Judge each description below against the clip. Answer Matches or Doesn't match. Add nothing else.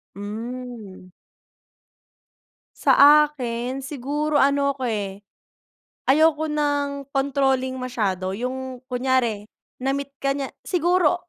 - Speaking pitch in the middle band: Doesn't match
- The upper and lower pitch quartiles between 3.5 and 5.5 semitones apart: Doesn't match